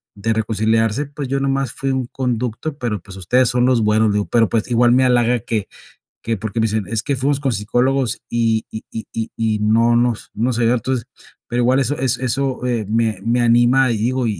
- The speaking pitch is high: No, low, 120 Hz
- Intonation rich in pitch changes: No, narrow, 2.6 semitones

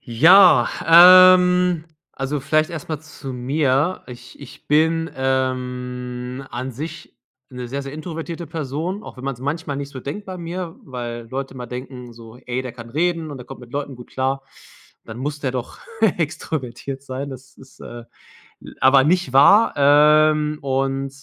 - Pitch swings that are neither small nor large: Yes, average, 3.6 semitones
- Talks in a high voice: No, low, 135 Hz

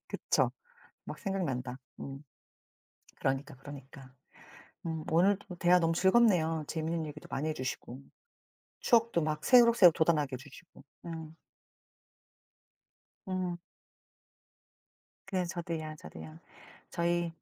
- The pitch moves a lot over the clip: No, average, 3.9 semitones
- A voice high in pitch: No, medium, 160 Hz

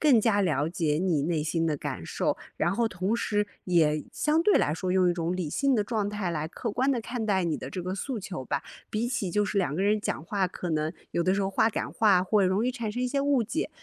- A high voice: Yes, high, 195 Hz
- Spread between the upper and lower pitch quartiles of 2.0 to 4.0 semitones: No, average, 4.7 semitones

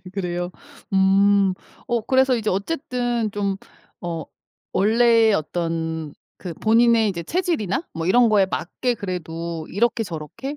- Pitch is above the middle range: Yes, high, 200 Hz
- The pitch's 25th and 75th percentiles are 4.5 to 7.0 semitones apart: Yes, average, 5.2 semitones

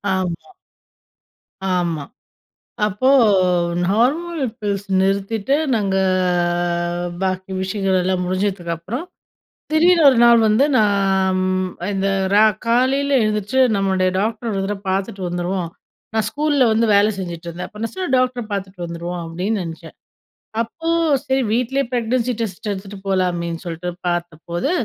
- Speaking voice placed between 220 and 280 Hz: No, high, 195 Hz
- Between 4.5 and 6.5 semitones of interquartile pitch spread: No, average, 4.1 semitones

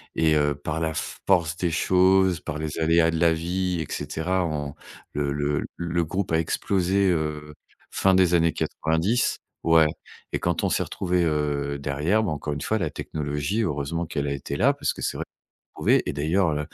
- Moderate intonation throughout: Yes, average, 3.2 semitones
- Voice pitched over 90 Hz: No, very low, 80 Hz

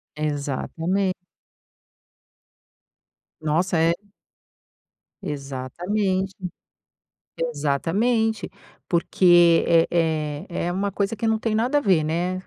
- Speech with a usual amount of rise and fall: Yes, average, 4.2 semitones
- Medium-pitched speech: Yes, medium, 175 Hz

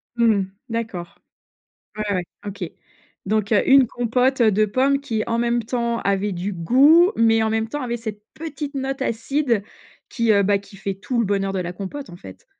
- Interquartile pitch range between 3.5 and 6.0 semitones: Yes, average, 4.2 semitones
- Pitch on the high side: Yes, high, 225 Hz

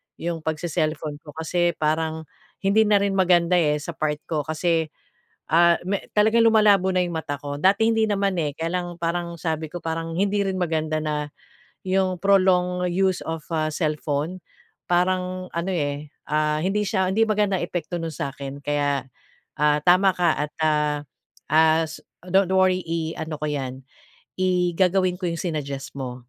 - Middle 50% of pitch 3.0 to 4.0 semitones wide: Yes, average, 3.4 semitones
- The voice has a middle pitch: Yes, medium, 170 Hz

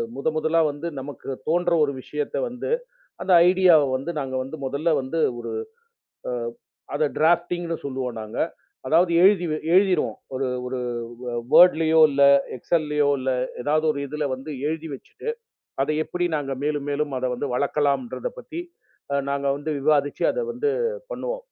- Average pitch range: Yes, average, 3.6 semitones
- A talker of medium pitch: Yes, medium, 150 Hz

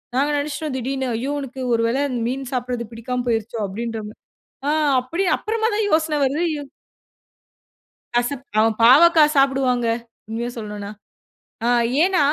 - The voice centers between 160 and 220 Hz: No, very high, 260 Hz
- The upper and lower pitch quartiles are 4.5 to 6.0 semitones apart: No, average, 3.7 semitones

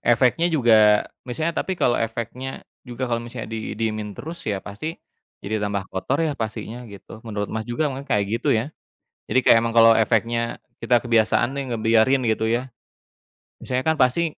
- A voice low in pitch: Yes, low, 115 Hz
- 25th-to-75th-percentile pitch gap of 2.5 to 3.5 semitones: Yes, average, 2.9 semitones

